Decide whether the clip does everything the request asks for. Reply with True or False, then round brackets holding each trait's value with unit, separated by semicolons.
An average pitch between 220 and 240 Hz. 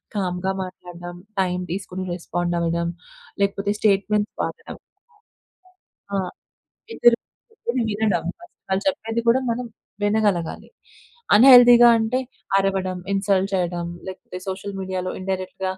False (195 Hz)